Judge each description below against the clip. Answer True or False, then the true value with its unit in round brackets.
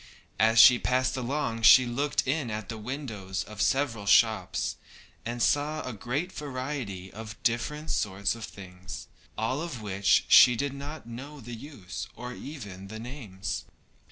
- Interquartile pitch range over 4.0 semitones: True (4.7 semitones)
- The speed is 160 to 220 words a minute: False (150 wpm)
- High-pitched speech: False (120 Hz)